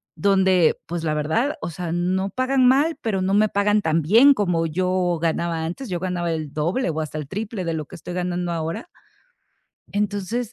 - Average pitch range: Yes, average, 4.0 semitones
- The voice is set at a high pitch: No, medium, 180 Hz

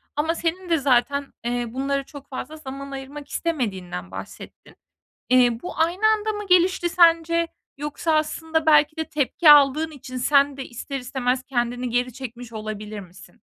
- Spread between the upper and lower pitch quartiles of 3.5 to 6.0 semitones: Yes, average, 4.6 semitones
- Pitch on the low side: No, very high, 275 Hz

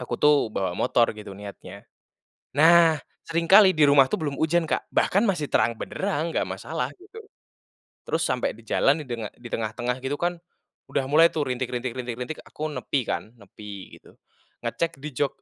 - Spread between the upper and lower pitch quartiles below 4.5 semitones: No, average, 5.3 semitones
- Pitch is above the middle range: No, medium, 140 Hz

